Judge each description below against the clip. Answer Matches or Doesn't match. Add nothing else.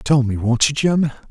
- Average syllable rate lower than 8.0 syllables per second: Matches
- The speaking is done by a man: Matches